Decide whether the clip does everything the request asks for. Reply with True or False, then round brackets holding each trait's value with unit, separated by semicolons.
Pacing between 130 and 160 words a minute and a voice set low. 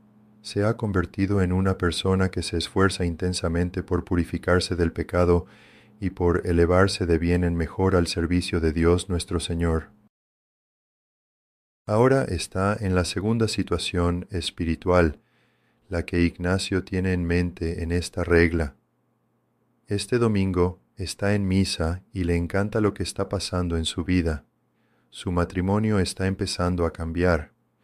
True (140 wpm; 90 Hz)